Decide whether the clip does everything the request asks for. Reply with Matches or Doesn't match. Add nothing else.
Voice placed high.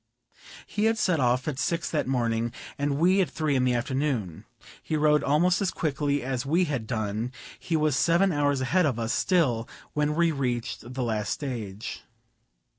Doesn't match